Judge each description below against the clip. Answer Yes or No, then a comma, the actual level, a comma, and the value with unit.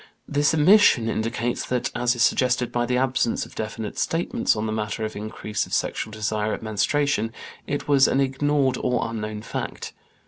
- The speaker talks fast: No, average, 175 wpm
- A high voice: No, low, 120 Hz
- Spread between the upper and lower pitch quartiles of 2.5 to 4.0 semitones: Yes, average, 3.7 semitones